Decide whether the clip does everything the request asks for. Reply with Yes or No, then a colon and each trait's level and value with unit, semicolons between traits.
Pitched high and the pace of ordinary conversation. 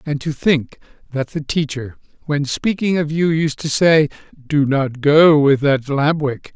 No: medium, 145 Hz; average, 185 wpm